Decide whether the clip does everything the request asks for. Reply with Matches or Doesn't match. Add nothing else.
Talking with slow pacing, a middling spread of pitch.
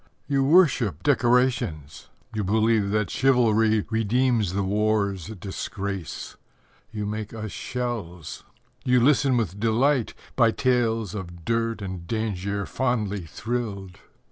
Matches